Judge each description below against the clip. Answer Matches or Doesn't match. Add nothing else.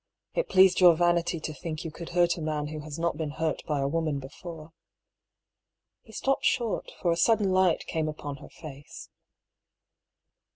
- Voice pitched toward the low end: Doesn't match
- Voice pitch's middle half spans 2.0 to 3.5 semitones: Matches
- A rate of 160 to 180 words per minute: Matches